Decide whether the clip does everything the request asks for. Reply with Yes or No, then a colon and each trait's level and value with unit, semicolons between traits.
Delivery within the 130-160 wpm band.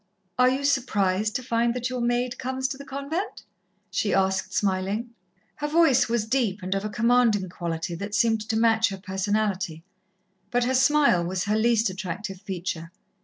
No: average, 170 wpm